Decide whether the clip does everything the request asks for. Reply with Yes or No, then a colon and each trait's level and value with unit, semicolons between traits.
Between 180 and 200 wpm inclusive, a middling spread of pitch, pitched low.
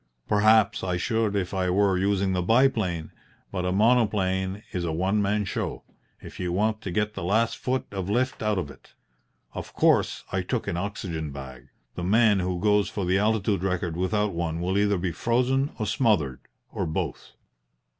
Yes: average, 185 wpm; average, 3.1 semitones; very low, 95 Hz